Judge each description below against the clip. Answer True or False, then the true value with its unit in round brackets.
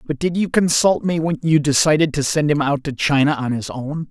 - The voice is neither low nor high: True (150 Hz)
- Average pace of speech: False (250 wpm)